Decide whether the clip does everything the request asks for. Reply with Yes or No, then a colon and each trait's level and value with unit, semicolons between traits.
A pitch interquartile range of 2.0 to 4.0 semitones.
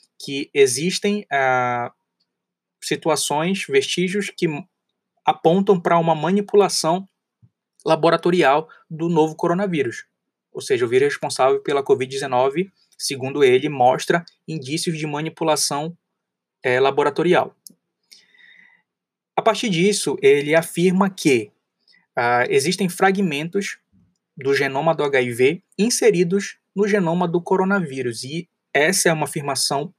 No: wide, 5.6 semitones